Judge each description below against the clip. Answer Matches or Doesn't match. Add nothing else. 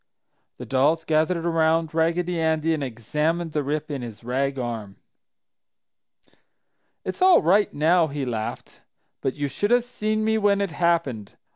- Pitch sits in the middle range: Matches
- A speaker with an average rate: Matches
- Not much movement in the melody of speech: Doesn't match